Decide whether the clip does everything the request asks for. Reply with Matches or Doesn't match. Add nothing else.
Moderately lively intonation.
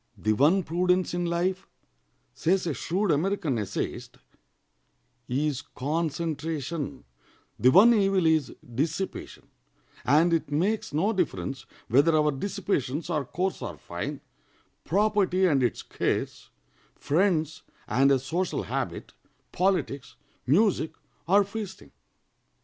Matches